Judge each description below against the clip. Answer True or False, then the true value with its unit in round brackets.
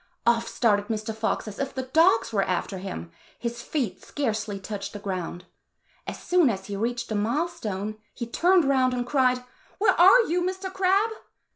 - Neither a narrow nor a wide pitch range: False (7.7 semitones)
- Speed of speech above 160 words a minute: True (180 wpm)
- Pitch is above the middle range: True (235 Hz)